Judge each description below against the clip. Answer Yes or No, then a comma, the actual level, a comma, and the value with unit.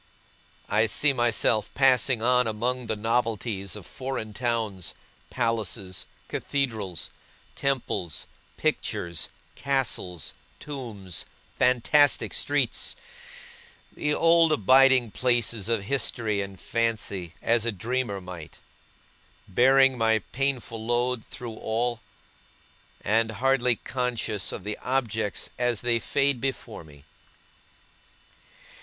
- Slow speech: Yes, slow, 100 wpm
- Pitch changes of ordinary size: Yes, average, 3.4 semitones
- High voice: No, low, 115 Hz